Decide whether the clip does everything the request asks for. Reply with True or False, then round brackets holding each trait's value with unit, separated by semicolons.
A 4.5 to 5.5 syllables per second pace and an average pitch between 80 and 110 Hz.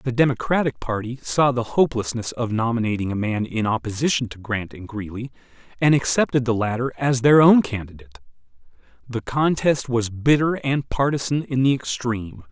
False (5.4 syllables/s; 125 Hz)